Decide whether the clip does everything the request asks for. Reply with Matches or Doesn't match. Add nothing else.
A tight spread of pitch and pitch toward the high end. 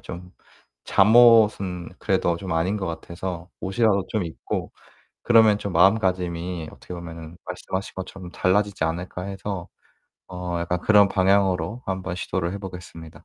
Doesn't match